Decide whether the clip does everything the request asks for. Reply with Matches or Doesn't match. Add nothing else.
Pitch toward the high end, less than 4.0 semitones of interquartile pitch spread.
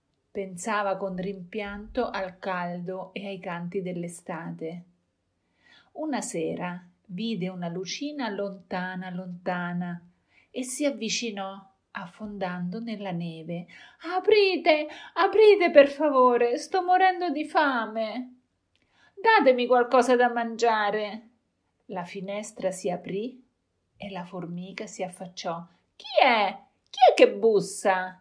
Doesn't match